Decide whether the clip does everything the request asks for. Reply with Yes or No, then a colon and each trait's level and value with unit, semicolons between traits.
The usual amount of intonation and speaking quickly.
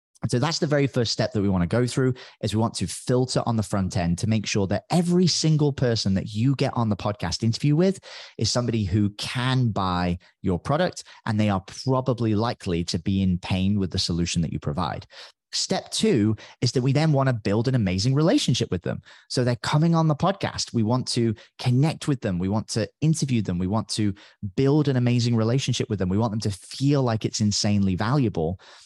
Yes: average, 4.6 semitones; fast, 225 wpm